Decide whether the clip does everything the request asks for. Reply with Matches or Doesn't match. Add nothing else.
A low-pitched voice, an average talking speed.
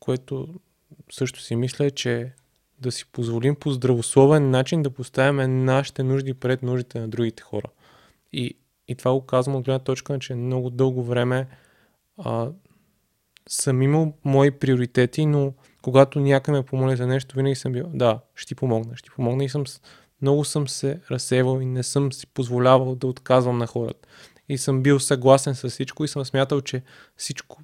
Doesn't match